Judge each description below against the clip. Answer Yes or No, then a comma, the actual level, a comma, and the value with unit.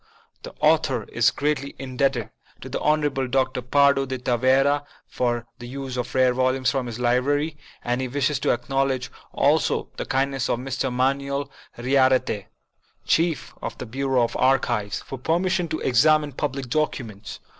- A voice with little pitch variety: Yes, narrow, 2.2 semitones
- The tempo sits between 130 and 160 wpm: Yes, average, 155 wpm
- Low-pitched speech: Yes, low, 130 Hz